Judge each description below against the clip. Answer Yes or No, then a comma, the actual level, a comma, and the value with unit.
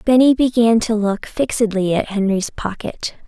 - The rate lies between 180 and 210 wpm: No, average, 145 wpm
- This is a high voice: Yes, high, 220 Hz